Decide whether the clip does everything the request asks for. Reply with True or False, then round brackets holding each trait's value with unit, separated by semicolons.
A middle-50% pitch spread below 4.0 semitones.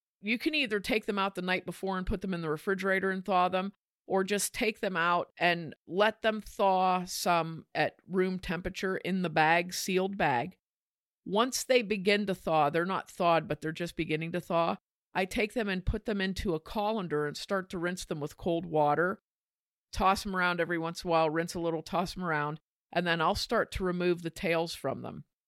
True (2.8 semitones)